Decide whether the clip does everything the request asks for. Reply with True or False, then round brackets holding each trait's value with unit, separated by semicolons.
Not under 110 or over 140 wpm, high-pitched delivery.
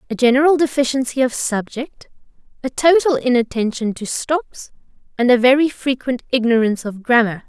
True (135 wpm; 255 Hz)